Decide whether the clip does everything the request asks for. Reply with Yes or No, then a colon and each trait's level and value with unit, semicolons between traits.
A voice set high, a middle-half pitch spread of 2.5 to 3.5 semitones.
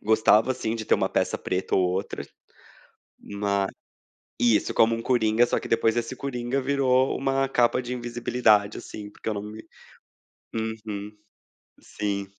No: low, 115 Hz; average, 2.9 semitones